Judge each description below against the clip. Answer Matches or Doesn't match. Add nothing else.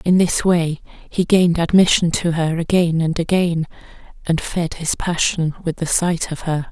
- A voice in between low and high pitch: Matches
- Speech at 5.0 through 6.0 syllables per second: Doesn't match